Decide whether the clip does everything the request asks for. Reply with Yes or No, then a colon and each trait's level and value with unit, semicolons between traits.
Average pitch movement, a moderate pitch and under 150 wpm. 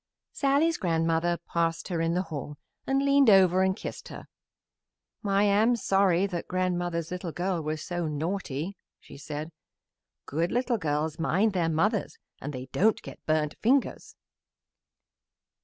Yes: average, 3.6 semitones; medium, 175 Hz; average, 140 wpm